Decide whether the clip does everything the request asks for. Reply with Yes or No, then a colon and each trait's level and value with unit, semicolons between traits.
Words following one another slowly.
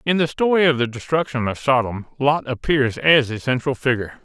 No: average, 200 wpm